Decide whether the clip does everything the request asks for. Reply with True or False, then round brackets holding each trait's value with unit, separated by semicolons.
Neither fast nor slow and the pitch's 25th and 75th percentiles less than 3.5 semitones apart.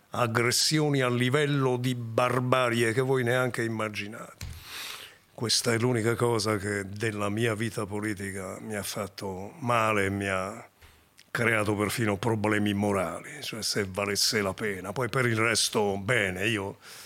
True (140 wpm; 3.1 semitones)